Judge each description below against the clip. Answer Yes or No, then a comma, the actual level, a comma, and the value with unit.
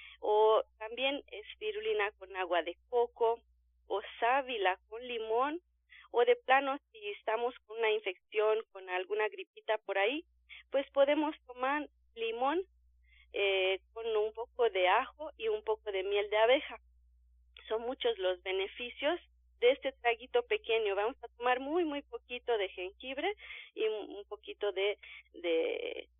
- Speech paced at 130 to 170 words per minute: Yes, average, 140 wpm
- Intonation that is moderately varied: No, wide, 5.8 semitones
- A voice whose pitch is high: Yes, high, 230 Hz